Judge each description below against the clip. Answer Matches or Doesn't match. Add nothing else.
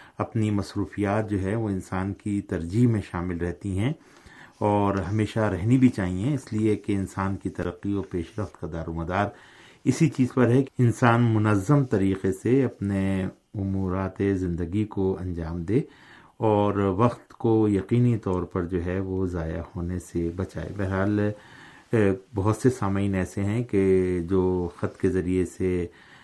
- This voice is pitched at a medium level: Doesn't match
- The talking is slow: Doesn't match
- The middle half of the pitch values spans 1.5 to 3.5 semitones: Matches